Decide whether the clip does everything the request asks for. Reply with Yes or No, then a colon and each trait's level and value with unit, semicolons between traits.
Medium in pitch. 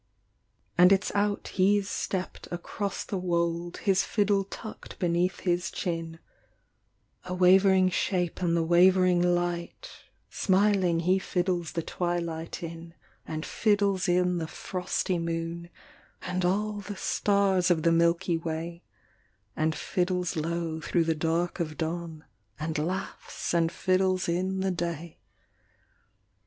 Yes: medium, 175 Hz